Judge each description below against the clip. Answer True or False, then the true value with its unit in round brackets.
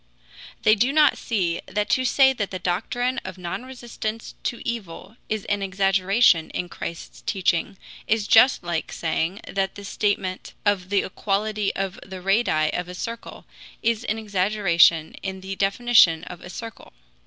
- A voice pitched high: True (195 Hz)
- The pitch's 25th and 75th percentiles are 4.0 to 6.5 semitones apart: False (3.5 semitones)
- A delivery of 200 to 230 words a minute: False (160 wpm)